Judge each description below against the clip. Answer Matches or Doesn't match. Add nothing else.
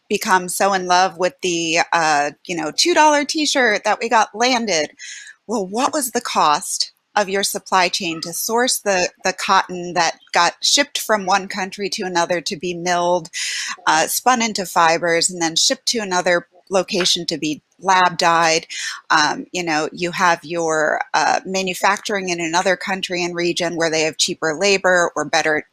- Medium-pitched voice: Matches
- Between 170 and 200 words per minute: Matches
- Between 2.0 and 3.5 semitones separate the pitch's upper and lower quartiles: Matches